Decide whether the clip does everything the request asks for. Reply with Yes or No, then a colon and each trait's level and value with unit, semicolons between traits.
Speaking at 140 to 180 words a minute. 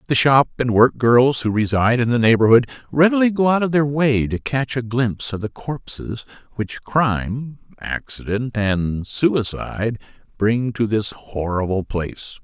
Yes: average, 160 wpm